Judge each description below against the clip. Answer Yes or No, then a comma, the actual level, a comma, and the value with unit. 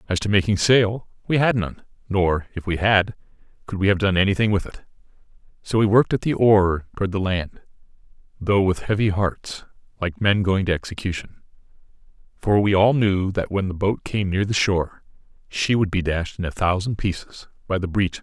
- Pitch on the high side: No, low, 100 Hz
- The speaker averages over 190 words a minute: Yes, fast, 205 wpm